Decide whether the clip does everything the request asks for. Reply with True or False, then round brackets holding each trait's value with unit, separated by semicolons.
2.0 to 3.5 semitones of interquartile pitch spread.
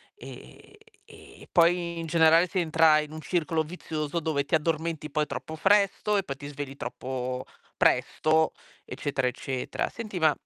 True (2.7 semitones)